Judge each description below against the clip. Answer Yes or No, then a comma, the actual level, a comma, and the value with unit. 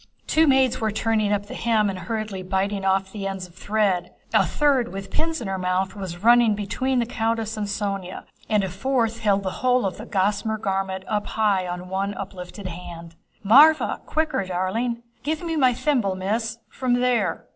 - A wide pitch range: No, average, 3.8 semitones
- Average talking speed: Yes, average, 190 wpm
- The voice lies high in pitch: Yes, high, 205 Hz